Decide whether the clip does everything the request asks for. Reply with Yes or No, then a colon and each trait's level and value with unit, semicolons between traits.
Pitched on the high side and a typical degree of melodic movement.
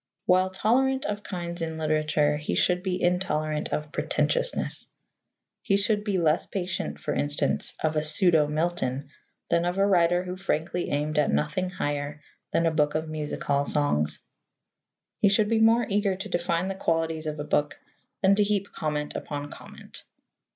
No: medium, 170 Hz; average, 4.1 semitones